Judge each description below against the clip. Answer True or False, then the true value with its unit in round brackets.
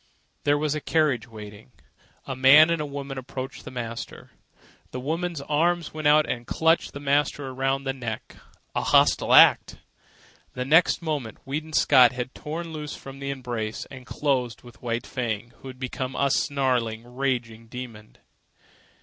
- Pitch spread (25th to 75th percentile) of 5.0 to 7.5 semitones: False (3.3 semitones)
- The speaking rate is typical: True (160 wpm)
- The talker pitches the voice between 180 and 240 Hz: False (135 Hz)